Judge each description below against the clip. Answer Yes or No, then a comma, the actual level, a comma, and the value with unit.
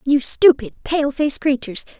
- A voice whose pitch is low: No, very high, 280 Hz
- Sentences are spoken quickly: No, average, 150 wpm